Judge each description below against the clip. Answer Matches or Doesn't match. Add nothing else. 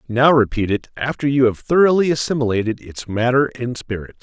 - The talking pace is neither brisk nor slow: Matches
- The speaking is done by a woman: Doesn't match